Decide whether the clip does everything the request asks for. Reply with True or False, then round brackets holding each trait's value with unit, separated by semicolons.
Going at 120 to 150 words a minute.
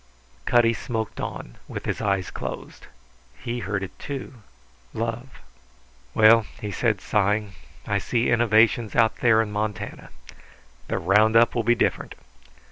True (135 wpm)